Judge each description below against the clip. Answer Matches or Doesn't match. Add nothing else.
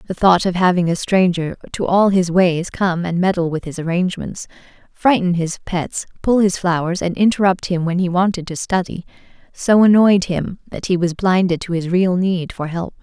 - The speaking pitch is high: Doesn't match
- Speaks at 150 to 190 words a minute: Doesn't match